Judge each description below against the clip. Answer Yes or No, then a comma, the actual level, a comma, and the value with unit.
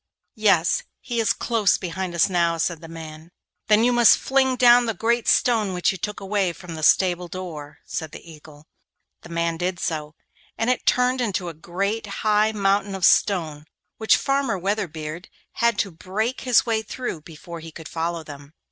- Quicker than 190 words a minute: No, average, 185 wpm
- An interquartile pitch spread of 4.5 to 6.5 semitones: Yes, average, 5.0 semitones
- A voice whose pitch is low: No, medium, 185 Hz